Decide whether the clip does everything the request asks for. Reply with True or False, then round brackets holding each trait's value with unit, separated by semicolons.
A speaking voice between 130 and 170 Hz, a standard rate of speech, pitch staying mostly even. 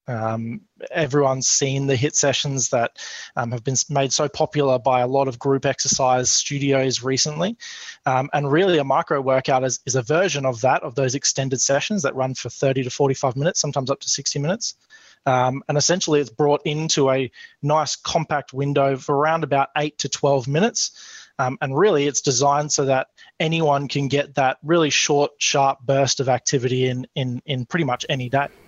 True (140 Hz; 190 wpm; 2.2 semitones)